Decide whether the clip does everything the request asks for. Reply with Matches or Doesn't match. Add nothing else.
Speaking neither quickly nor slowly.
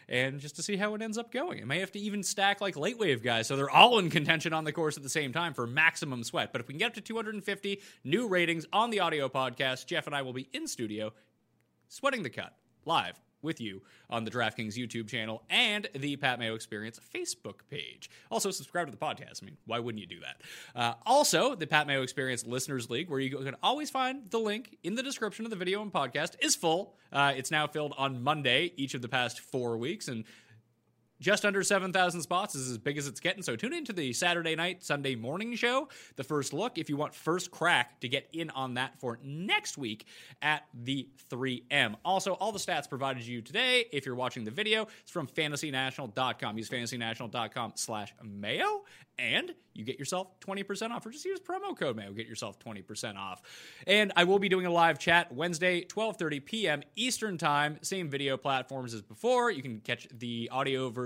Doesn't match